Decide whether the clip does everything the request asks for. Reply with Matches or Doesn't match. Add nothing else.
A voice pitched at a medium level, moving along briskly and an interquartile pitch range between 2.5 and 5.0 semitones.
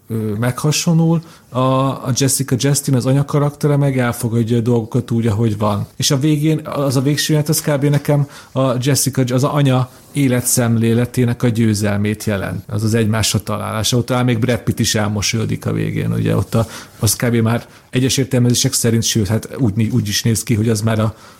Doesn't match